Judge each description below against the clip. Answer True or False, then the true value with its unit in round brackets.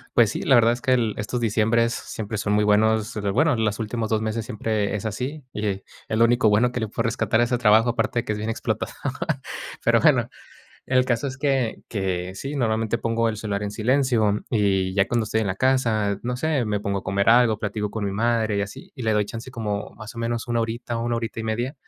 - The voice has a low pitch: True (110 Hz)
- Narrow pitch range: True (2.3 semitones)